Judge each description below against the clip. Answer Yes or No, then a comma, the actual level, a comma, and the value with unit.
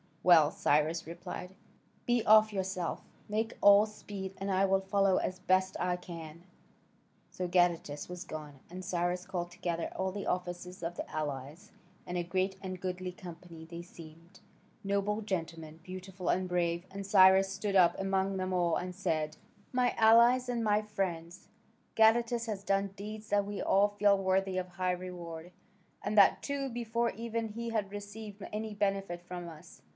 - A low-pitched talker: No, high, 190 Hz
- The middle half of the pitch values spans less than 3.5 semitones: Yes, average, 2.8 semitones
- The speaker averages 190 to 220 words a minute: No, average, 165 wpm